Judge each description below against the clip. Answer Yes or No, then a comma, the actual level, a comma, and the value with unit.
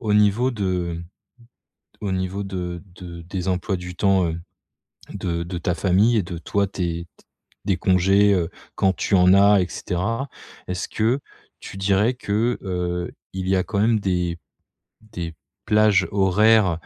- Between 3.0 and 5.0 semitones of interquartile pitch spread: No, narrow, 2.5 semitones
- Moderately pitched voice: No, very low, 95 Hz